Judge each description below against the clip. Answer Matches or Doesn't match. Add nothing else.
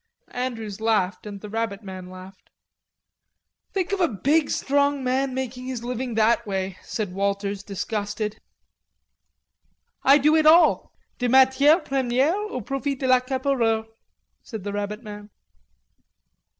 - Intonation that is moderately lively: Matches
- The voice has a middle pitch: Doesn't match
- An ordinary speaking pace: Doesn't match